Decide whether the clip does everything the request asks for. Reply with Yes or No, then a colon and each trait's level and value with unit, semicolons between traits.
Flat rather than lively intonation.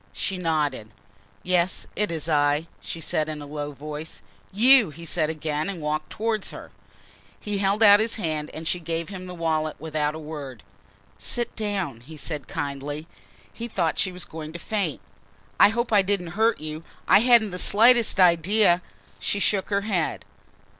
No: average, 4.9 semitones